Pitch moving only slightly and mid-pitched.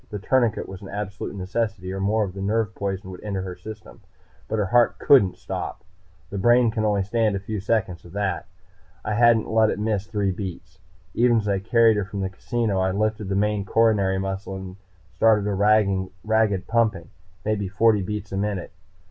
No: narrow, 2.3 semitones; low, 105 Hz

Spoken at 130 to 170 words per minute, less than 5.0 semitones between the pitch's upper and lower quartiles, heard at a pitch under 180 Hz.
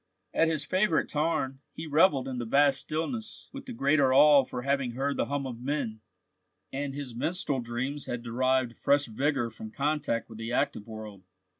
No: average, 180 wpm; average, 3.6 semitones; low, 135 Hz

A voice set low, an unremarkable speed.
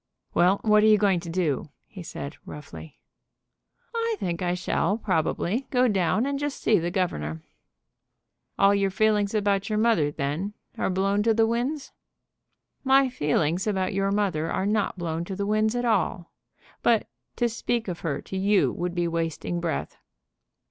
No: high, 195 Hz; average, 170 wpm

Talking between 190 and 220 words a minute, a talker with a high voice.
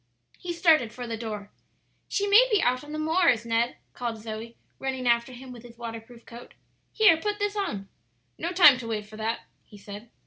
Yes: average, 200 wpm; high, 240 Hz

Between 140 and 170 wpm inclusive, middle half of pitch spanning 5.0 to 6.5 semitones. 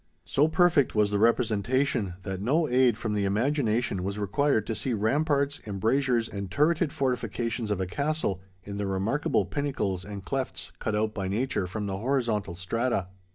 Yes: average, 165 wpm; average, 5.3 semitones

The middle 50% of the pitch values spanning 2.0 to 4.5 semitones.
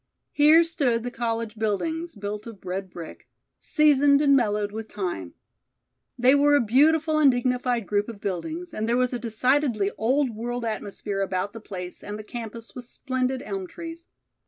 No: average, 5.1 semitones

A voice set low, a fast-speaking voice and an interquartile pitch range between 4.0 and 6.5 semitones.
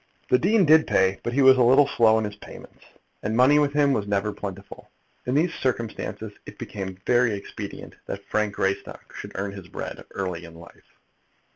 No: low, 110 Hz; average, 195 wpm; average, 5.2 semitones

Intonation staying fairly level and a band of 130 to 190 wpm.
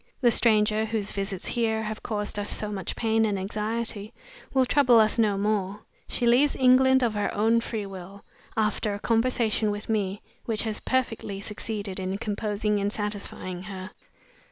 Yes: narrow, 2.0 semitones; average, 165 wpm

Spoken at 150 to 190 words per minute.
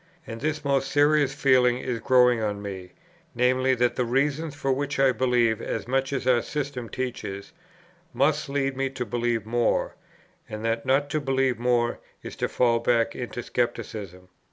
Yes: average, 170 wpm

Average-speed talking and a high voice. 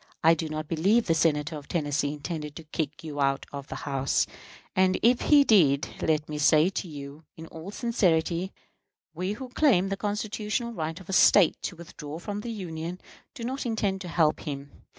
No: average, 190 wpm; medium, 165 Hz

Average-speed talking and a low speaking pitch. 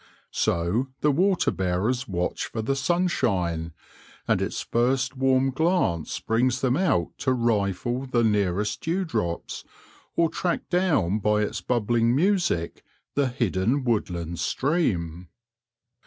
No: slow, 120 wpm; low, 120 Hz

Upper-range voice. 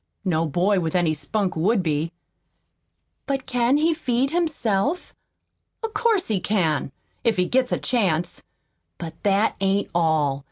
Yes: high, 200 Hz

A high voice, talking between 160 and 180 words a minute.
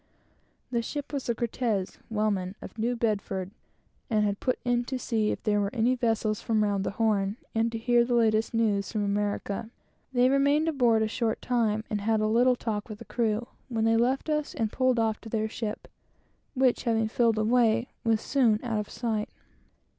No: high, 225 Hz; average, 195 wpm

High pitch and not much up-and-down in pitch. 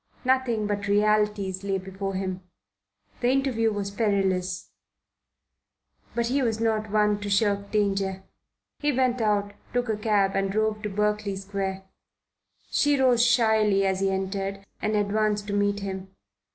Yes: high, 205 Hz; narrow, 2.0 semitones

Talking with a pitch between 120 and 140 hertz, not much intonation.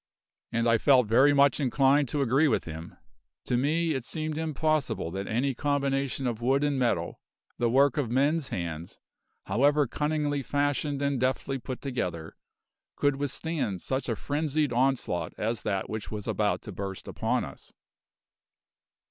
No: low, 135 Hz; average, 3.7 semitones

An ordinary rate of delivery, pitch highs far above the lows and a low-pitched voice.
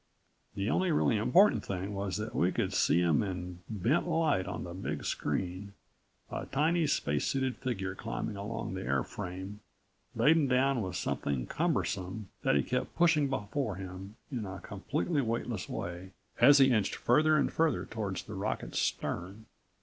Yes: average, 155 wpm; wide, 6.3 semitones; low, 105 Hz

